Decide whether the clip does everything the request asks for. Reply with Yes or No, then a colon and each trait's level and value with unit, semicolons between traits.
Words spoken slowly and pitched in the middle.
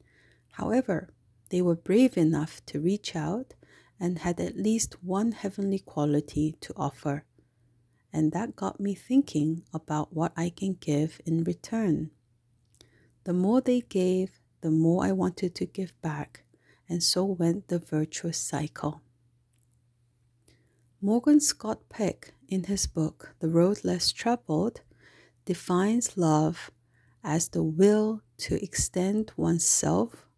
Yes: slow, 125 wpm; medium, 170 Hz